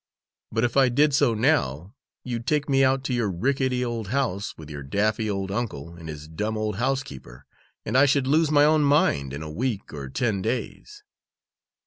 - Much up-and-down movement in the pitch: Yes, wide, 6.8 semitones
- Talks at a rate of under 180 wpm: No, average, 190 wpm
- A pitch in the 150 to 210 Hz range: No, low, 115 Hz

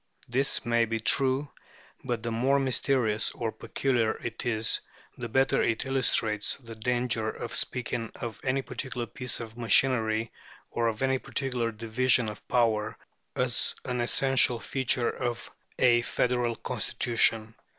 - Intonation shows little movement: Yes, narrow, 2.3 semitones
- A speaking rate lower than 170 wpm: Yes, average, 140 wpm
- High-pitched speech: No, low, 120 Hz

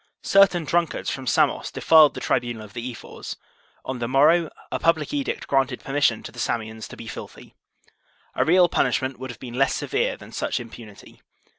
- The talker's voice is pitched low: Yes, low, 130 Hz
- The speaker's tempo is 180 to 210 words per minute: Yes, average, 185 wpm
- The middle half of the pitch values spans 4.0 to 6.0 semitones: Yes, average, 5.1 semitones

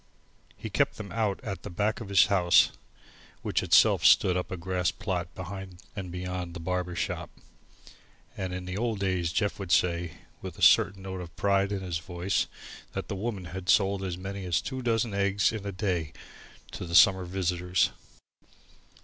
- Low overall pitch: Yes, very low, 95 Hz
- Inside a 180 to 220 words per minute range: Yes, average, 185 wpm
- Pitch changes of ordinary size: No, narrow, 1.8 semitones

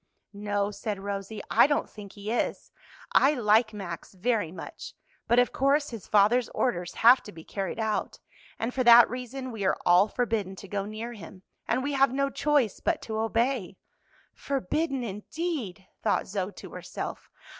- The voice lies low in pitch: No, high, 220 Hz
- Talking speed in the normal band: Yes, average, 170 wpm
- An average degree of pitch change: Yes, average, 4.2 semitones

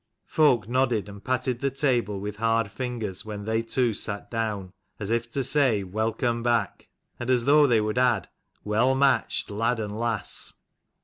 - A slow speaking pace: No, average, 180 wpm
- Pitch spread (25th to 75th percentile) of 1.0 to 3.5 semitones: Yes, average, 3.1 semitones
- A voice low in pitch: Yes, low, 115 Hz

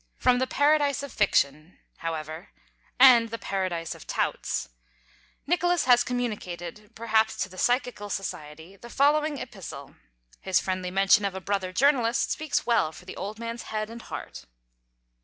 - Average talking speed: Yes, average, 150 wpm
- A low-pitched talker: No, high, 215 Hz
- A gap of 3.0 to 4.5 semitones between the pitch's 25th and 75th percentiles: No, average, 5.1 semitones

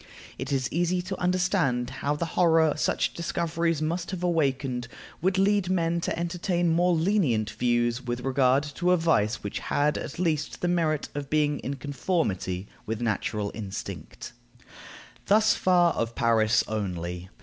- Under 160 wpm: Yes, average, 150 wpm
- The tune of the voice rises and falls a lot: Yes, wide, 6.3 semitones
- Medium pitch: Yes, medium, 155 Hz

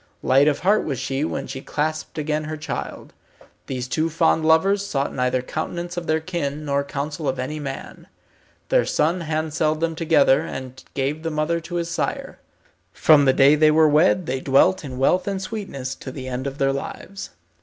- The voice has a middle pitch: Yes, medium, 155 Hz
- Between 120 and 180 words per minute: No, average, 195 wpm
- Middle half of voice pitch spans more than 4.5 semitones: No, average, 3.2 semitones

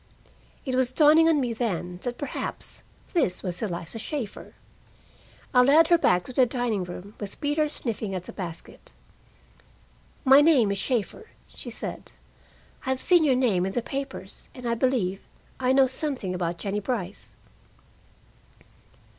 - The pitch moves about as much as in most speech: No, wide, 5.8 semitones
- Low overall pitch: No, high, 245 Hz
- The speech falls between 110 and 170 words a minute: Yes, average, 150 wpm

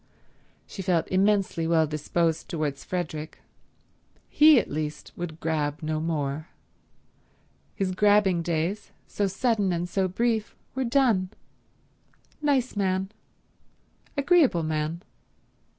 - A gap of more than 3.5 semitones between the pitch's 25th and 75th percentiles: Yes, average, 4.7 semitones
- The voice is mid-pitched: Yes, medium, 180 Hz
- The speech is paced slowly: Yes, slow, 105 wpm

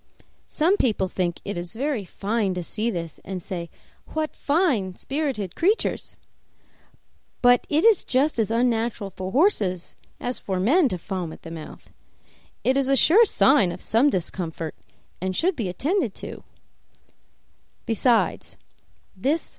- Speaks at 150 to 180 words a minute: No, slow, 135 wpm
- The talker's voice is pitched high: Yes, high, 225 Hz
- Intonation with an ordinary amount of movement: No, wide, 7.7 semitones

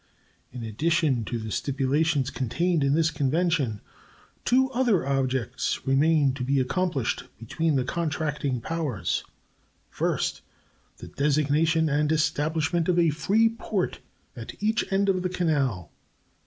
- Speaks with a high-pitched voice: No, medium, 150 Hz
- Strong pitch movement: No, average, 4.2 semitones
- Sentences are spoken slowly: Yes, slow, 130 wpm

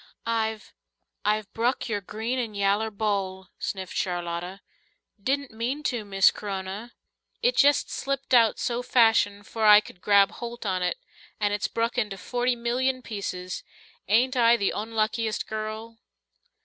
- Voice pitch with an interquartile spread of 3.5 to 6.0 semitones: No, average, 3.0 semitones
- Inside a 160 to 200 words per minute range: No, average, 145 wpm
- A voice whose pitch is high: Yes, high, 220 Hz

